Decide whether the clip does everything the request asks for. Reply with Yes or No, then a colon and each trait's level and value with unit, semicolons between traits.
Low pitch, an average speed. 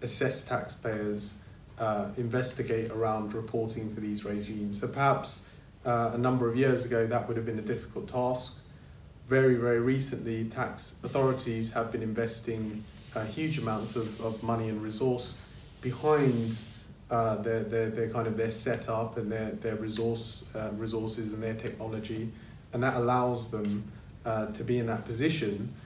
Yes: low, 115 Hz; average, 160 wpm